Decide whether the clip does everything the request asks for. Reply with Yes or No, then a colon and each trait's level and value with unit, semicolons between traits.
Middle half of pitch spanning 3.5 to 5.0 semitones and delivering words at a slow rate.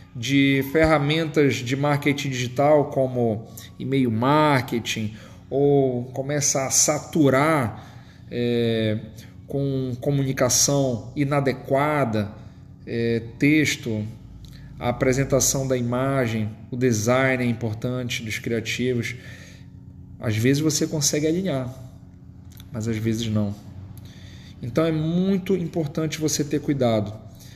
Yes: average, 4.1 semitones; slow, 95 wpm